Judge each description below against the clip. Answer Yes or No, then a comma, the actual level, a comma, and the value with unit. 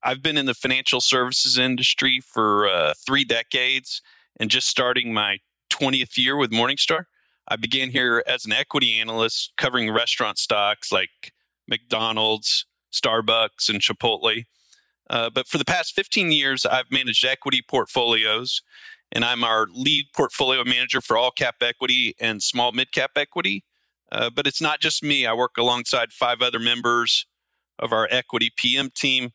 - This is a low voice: Yes, low, 125 Hz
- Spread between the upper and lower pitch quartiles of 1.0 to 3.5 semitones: Yes, average, 3.1 semitones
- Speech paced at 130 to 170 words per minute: Yes, average, 155 wpm